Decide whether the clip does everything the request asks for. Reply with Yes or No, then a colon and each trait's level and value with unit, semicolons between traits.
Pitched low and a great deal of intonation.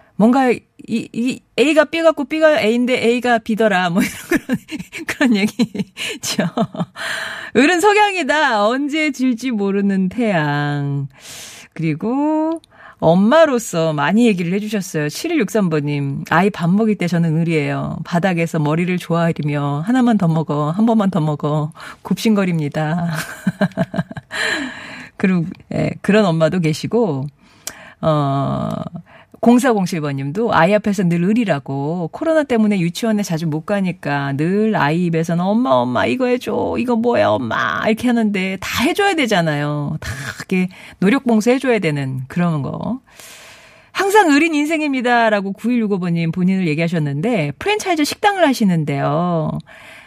No: high, 200 Hz; wide, 6.8 semitones